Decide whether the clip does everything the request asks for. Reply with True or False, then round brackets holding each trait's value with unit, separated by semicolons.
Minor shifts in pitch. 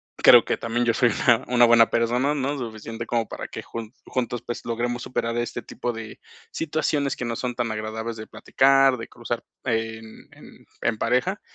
True (1.8 semitones)